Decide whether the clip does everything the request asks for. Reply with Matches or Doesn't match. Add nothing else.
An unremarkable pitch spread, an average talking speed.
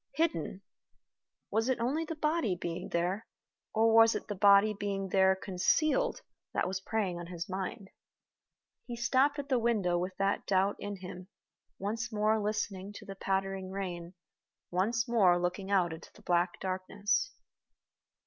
Matches